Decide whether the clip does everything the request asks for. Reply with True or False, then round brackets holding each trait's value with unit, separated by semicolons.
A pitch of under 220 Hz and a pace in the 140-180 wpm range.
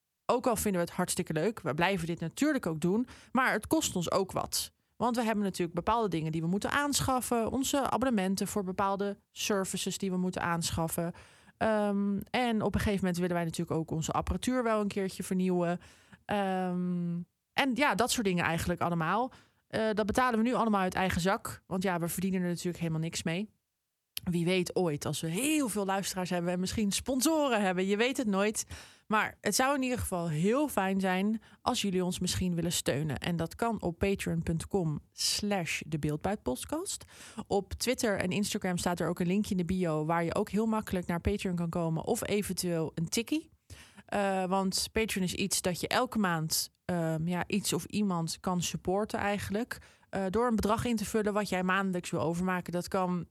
False (190 Hz; 195 wpm)